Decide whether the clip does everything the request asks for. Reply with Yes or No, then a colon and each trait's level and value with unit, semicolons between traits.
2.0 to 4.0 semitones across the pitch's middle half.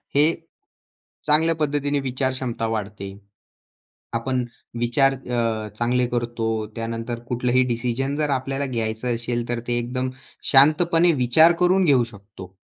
Yes: average, 3.1 semitones